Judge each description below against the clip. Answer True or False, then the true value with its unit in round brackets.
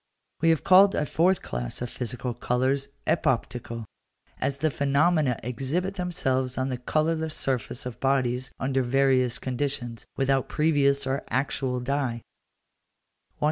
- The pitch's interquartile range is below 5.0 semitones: True (2.8 semitones)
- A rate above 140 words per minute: False (135 wpm)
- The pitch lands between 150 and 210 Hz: False (135 Hz)